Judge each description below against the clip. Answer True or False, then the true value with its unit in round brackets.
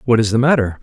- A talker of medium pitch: False (115 Hz)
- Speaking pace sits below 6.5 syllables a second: False (7.3 syllables/s)